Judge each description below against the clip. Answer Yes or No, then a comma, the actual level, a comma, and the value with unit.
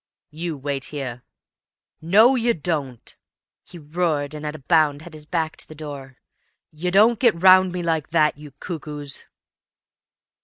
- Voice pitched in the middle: Yes, medium, 155 Hz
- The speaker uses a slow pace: No, average, 155 wpm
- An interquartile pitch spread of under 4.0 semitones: Yes, average, 3.4 semitones